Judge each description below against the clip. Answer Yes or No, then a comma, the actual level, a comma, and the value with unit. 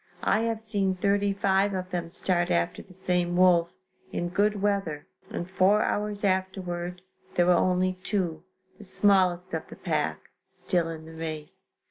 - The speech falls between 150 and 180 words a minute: Yes, average, 160 wpm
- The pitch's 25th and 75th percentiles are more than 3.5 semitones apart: No, narrow, 2.4 semitones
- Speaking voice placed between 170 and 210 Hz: Yes, medium, 185 Hz